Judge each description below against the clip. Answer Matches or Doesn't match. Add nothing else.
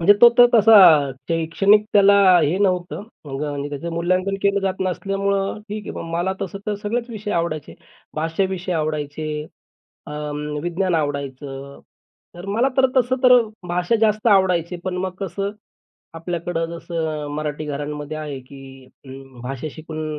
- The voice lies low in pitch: Doesn't match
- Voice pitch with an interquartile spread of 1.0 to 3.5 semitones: Doesn't match